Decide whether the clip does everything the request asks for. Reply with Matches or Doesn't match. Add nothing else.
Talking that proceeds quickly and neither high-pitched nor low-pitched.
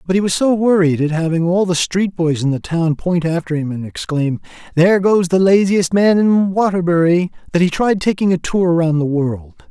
Matches